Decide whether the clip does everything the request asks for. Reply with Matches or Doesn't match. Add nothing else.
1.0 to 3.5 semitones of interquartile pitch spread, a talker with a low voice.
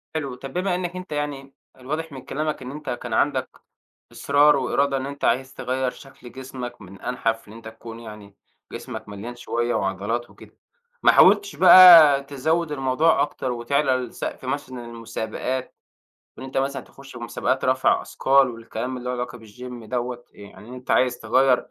Matches